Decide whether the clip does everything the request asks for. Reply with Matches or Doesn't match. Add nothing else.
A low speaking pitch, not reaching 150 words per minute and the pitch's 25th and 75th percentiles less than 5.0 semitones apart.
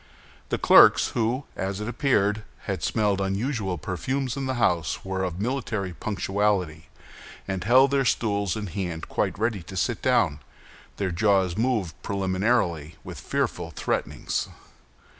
Matches